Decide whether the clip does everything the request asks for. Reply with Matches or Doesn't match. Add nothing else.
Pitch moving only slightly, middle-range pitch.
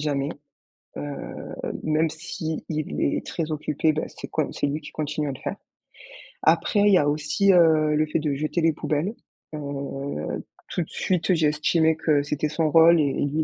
Matches